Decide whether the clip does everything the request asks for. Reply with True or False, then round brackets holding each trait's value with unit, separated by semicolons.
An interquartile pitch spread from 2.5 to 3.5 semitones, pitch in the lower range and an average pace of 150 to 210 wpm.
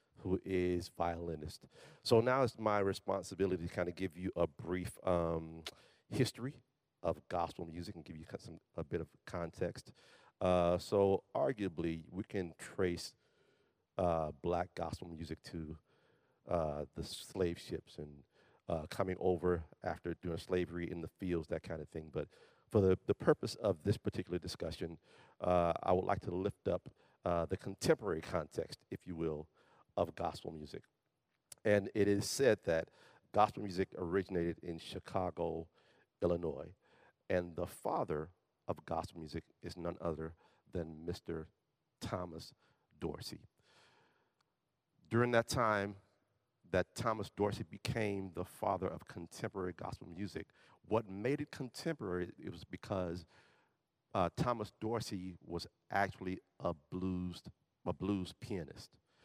False (3.2 semitones; 90 Hz; 140 wpm)